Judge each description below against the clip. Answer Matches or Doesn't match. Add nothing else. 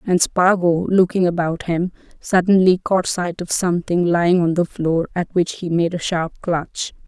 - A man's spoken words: Doesn't match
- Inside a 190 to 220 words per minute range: Doesn't match